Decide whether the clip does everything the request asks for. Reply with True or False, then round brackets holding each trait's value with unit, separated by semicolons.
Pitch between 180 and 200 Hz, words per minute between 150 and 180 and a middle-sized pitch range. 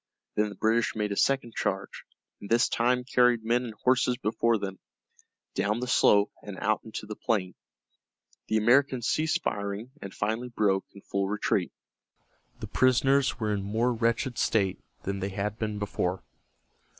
False (110 Hz; 160 wpm; 3.3 semitones)